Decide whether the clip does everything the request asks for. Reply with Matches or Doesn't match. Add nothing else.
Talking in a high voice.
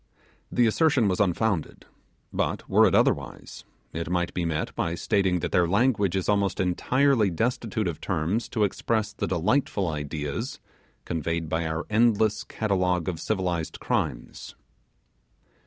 Doesn't match